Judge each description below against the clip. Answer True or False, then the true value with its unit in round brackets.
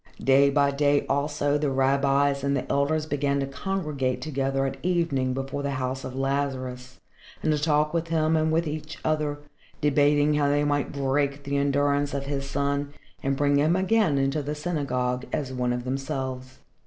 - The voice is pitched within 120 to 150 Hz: True (140 Hz)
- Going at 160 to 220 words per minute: True (180 wpm)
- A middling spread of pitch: False (1.6 semitones)